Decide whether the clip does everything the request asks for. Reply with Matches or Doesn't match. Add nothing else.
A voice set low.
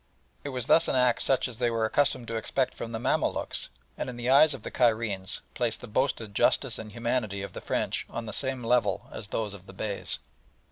Matches